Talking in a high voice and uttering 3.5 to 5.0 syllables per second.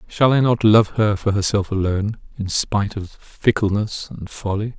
No: low, 105 Hz; 4.8 syllables/s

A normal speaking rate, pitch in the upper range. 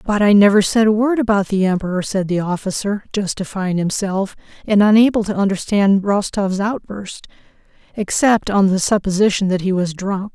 Yes: average, 160 wpm; high, 200 Hz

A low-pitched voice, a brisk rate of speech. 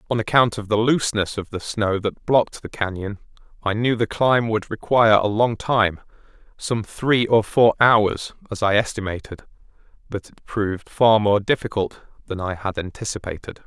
No: low, 110 Hz; average, 170 wpm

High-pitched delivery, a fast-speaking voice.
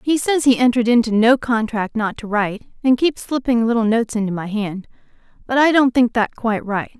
Yes: high, 235 Hz; fast, 215 wpm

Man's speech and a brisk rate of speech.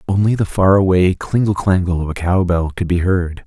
Yes: male; fast, 225 wpm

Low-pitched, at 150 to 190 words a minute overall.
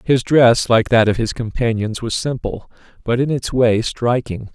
Yes: low, 120 Hz; average, 185 wpm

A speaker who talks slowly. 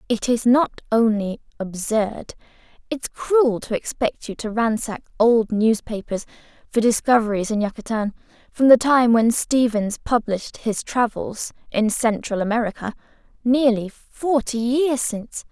Yes: slow, 125 wpm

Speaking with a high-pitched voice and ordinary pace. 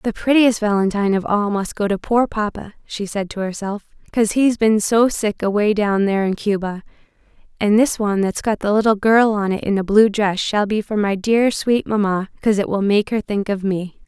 No: high, 210 Hz; fast, 225 wpm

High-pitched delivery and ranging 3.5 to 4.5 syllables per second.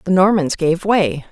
No: medium, 175 Hz; 4.3 syllables/s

